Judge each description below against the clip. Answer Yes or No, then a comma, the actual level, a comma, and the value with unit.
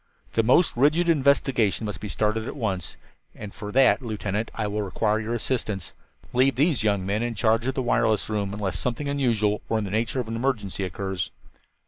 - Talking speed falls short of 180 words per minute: No, average, 195 wpm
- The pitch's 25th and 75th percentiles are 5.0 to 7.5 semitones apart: No, average, 3.5 semitones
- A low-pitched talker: Yes, low, 110 Hz